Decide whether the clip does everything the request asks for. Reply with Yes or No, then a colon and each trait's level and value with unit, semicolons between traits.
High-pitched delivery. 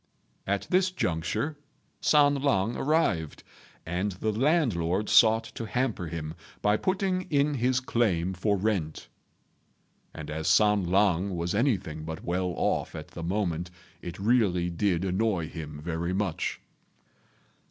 No: low, 100 Hz